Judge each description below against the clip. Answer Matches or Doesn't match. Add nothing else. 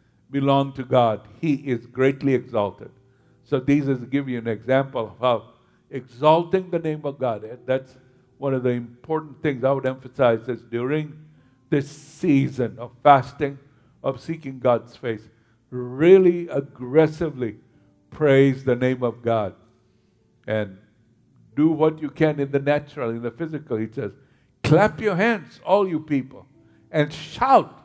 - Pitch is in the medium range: Doesn't match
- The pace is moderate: Matches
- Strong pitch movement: Doesn't match